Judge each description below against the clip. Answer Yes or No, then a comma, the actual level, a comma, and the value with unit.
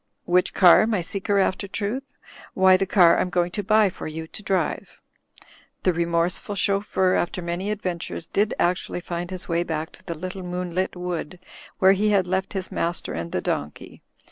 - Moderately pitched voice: Yes, medium, 180 Hz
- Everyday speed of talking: Yes, average, 180 wpm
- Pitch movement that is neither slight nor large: No, narrow, 2.2 semitones